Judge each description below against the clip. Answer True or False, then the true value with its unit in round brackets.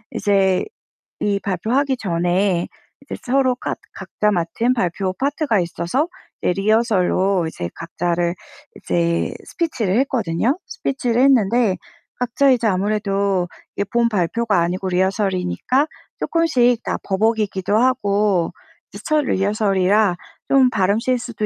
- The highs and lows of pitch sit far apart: False (4.9 semitones)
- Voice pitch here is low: False (205 Hz)